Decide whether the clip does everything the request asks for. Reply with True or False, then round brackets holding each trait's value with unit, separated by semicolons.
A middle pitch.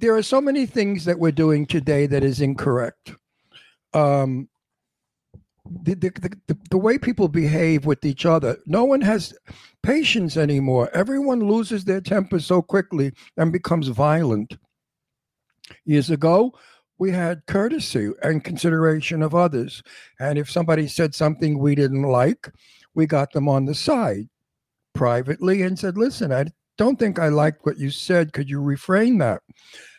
True (160 Hz)